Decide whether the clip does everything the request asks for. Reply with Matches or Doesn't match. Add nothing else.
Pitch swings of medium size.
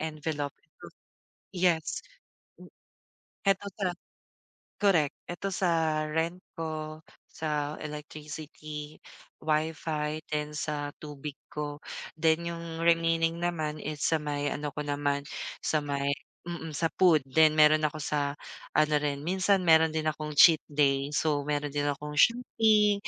Doesn't match